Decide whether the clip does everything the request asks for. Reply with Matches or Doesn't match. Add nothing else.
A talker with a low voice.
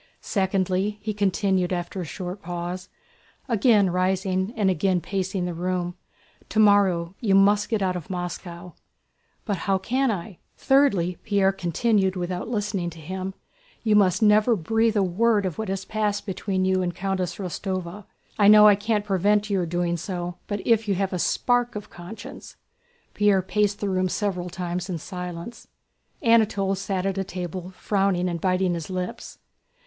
Doesn't match